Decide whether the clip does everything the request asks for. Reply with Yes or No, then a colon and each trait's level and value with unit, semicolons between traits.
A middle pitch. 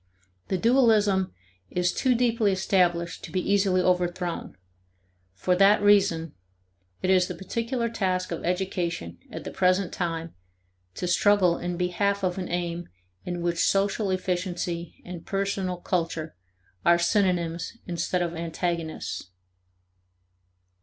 Yes: medium, 180 Hz